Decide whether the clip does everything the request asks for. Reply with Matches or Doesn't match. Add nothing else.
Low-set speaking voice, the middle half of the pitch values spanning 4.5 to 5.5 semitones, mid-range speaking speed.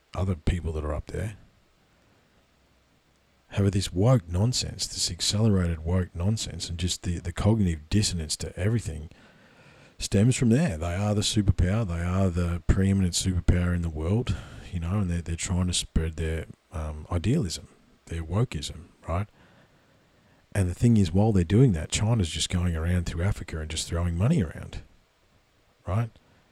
Doesn't match